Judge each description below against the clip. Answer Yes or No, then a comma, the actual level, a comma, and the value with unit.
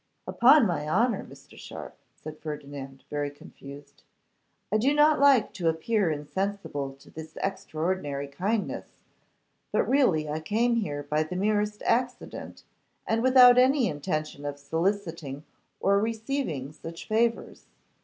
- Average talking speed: No, slow, 130 wpm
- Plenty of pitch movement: Yes, wide, 7.5 semitones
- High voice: No, medium, 180 Hz